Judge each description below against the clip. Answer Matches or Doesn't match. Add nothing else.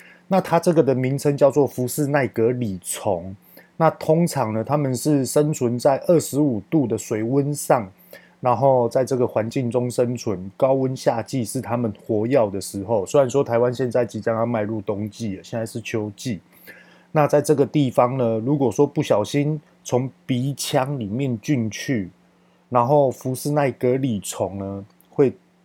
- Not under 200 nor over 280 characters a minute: Matches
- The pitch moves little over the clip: Doesn't match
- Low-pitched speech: Matches